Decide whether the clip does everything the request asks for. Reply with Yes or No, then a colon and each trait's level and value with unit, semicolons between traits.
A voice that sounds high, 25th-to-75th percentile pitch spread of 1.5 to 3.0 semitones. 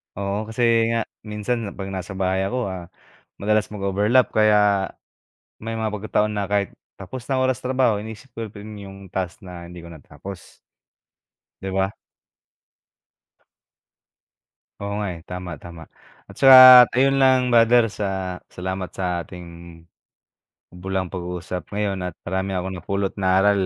No: low, 100 Hz; narrow, 2.5 semitones